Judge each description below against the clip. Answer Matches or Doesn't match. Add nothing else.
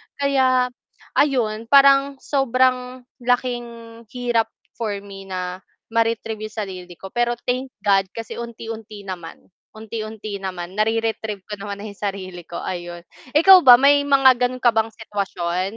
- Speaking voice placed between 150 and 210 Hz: Doesn't match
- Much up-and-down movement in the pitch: Doesn't match